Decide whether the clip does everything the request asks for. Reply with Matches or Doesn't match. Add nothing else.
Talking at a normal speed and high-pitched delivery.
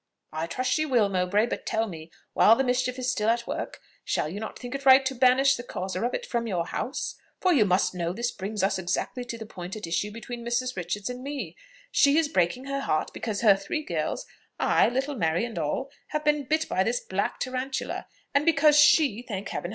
Doesn't match